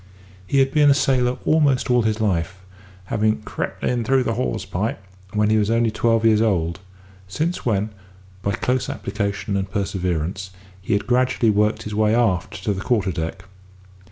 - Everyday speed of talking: Yes, average, 175 wpm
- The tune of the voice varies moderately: Yes, average, 3.9 semitones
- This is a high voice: No, low, 110 Hz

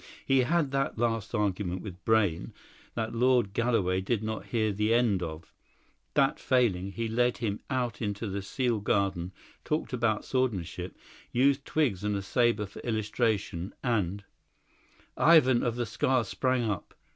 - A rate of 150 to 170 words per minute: Yes, average, 155 wpm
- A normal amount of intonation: Yes, average, 3.8 semitones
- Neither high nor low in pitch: No, low, 110 Hz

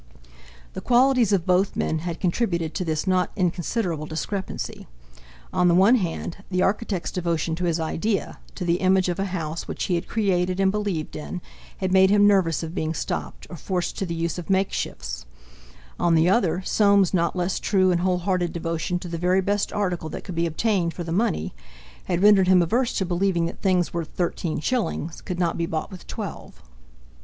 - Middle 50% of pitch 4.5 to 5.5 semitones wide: No, narrow, 2.5 semitones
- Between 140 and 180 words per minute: No, average, 190 wpm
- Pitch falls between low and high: Yes, medium, 180 Hz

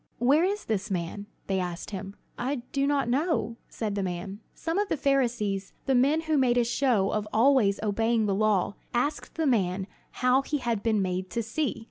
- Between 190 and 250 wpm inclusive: Yes, average, 195 wpm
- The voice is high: Yes, high, 230 Hz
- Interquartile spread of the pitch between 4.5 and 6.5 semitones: Yes, wide, 5.5 semitones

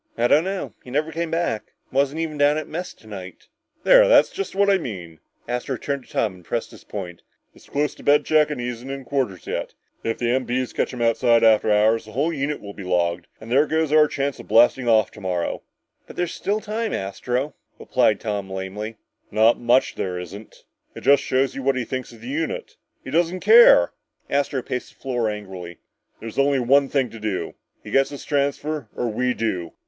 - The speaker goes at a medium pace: No, fast, 210 wpm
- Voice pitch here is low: Yes, low, 125 Hz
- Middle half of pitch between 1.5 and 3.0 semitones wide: No, average, 5.2 semitones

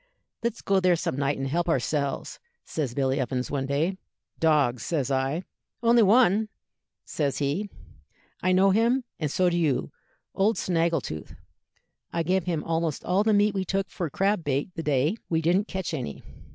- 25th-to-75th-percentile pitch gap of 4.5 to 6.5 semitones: Yes, wide, 5.4 semitones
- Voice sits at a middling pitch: Yes, medium, 165 Hz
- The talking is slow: No, average, 170 wpm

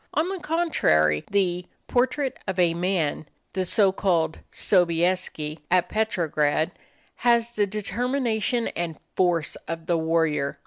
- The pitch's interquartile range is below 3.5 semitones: No, average, 5.2 semitones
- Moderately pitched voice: Yes, medium, 180 Hz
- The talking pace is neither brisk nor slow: No, slow, 125 wpm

